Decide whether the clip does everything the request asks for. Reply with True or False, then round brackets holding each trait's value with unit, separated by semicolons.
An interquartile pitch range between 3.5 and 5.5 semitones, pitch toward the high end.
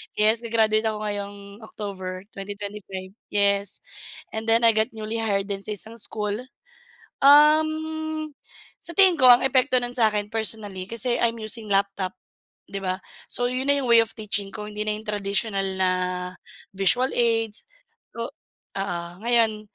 False (2.8 semitones; 215 Hz)